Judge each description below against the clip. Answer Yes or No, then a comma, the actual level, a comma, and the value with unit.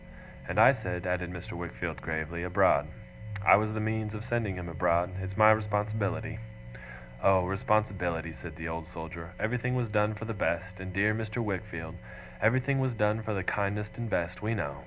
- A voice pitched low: Yes, low, 100 Hz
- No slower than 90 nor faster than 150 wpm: No, average, 180 wpm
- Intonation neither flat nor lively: Yes, average, 3.7 semitones